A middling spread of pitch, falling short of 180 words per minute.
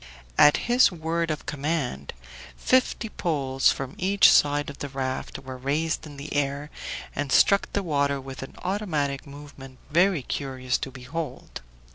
Yes: average, 3.4 semitones; average, 150 wpm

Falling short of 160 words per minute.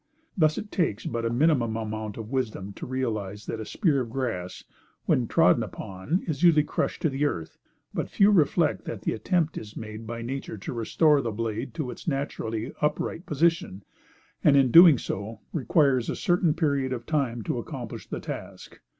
No: average, 185 wpm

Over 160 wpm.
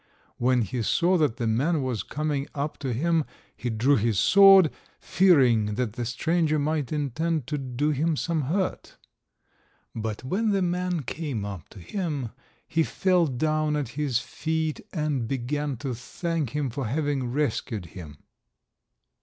No: average, 155 wpm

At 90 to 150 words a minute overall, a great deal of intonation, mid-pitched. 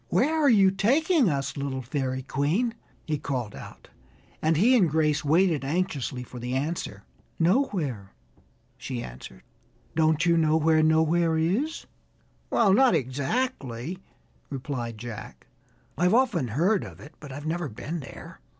Yes: average, 140 wpm; wide, 6.0 semitones; medium, 155 Hz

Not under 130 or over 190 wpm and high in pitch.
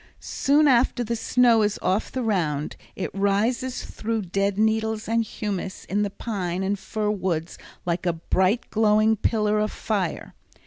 Yes: average, 165 wpm; high, 210 Hz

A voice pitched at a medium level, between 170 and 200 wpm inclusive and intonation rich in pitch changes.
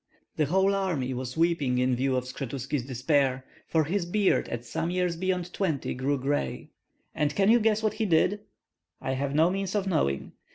Yes: medium, 155 Hz; average, 190 wpm; wide, 6.3 semitones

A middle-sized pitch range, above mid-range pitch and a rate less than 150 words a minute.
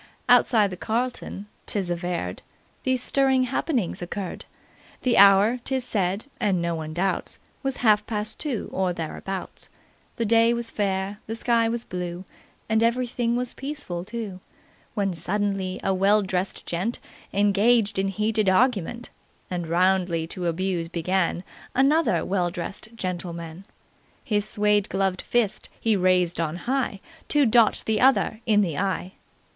Yes: average, 4.2 semitones; high, 200 Hz; average, 140 wpm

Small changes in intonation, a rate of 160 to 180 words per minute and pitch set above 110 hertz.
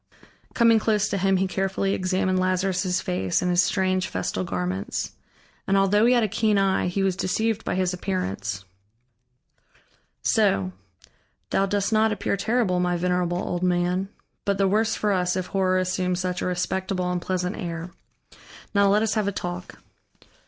Yes: narrow, 1.9 semitones; average, 165 wpm; medium, 185 Hz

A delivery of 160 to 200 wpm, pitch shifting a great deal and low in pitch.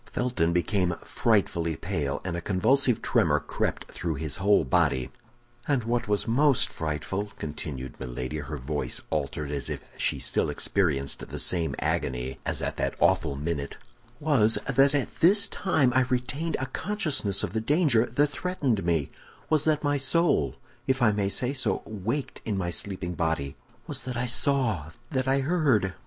Yes: average, 165 wpm; wide, 8.7 semitones; low, 105 Hz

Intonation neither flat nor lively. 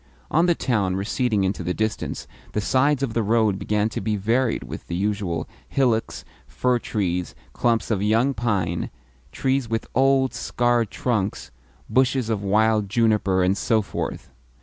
Yes: average, 3.5 semitones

